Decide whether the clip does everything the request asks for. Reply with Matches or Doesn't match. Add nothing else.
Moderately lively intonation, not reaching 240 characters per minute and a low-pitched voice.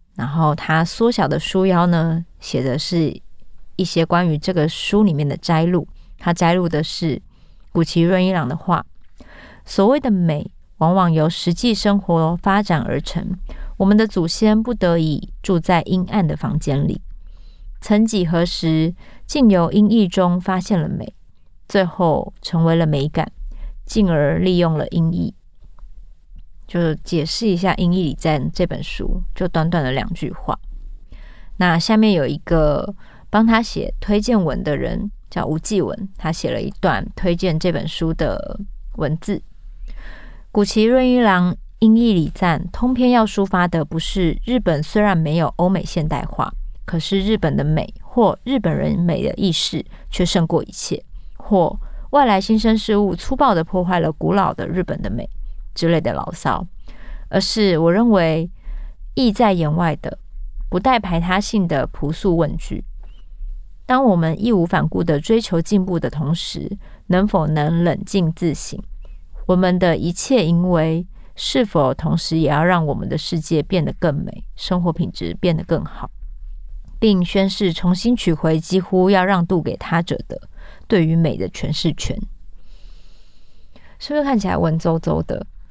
Doesn't match